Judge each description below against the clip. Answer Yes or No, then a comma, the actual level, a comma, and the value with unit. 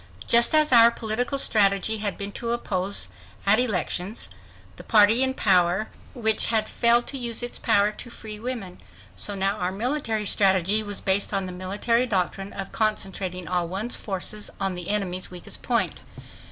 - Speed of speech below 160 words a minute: No, average, 165 wpm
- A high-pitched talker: Yes, high, 210 Hz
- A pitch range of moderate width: Yes, average, 3.4 semitones